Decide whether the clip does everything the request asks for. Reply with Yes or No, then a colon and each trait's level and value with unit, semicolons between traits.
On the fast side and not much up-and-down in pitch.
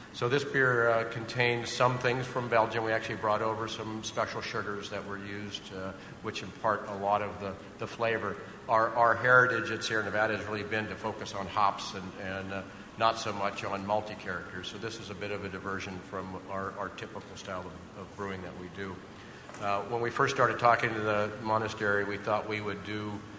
Yes: fast, 215 wpm; narrow, 2.2 semitones